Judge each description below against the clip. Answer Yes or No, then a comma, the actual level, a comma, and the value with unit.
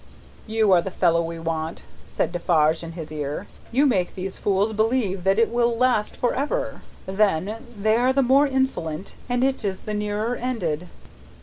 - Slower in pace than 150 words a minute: No, average, 180 wpm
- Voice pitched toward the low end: No, high, 205 Hz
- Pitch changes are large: Yes, wide, 6.0 semitones